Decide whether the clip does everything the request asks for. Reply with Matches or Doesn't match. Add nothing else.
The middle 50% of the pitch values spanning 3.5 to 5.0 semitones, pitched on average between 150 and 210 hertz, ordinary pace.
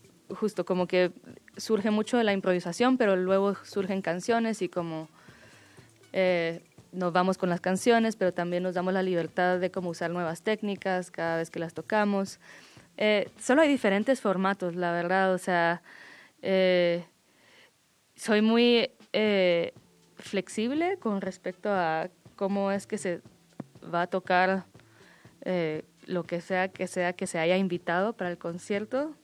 Doesn't match